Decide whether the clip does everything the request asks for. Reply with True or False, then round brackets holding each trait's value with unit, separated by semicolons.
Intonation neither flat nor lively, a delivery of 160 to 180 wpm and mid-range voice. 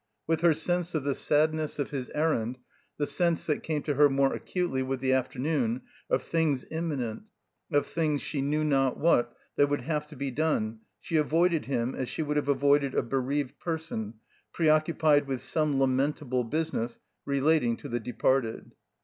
True (3.1 semitones; 175 wpm; 145 Hz)